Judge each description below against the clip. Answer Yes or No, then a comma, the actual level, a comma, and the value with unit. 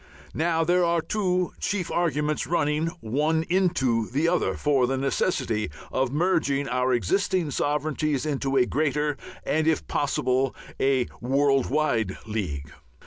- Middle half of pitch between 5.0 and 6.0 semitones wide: No, average, 3.9 semitones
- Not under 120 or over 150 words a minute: Yes, slow, 135 wpm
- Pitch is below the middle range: No, medium, 145 Hz